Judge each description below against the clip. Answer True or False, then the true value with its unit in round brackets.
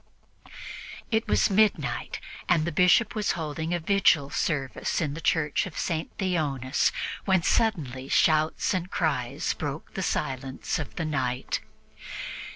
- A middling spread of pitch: True (4.8 semitones)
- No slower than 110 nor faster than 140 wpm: True (135 wpm)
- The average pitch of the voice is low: False (160 Hz)